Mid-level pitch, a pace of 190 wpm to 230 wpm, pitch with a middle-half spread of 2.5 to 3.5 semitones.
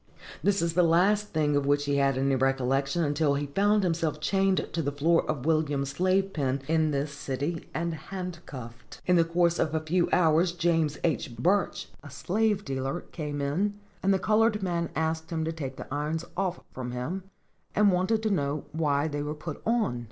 No: medium, 160 Hz; average, 195 wpm; average, 4.1 semitones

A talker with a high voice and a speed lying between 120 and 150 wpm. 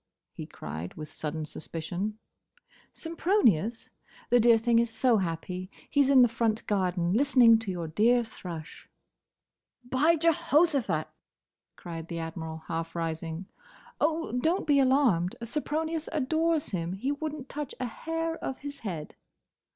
Yes: high, 230 Hz; average, 140 wpm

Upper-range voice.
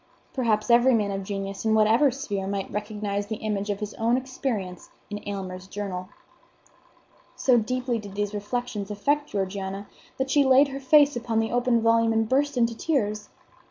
Yes: high, 220 Hz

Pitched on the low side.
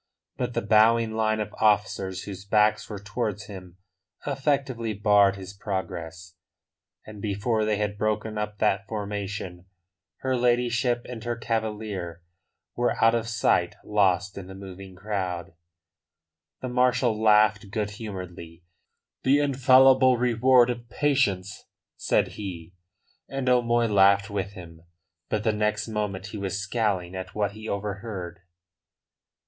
Yes: low, 105 Hz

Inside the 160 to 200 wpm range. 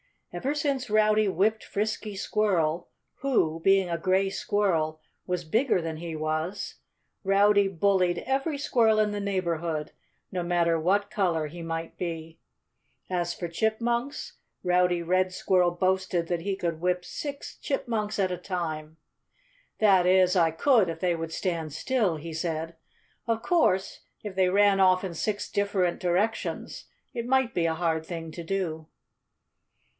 No: average, 150 wpm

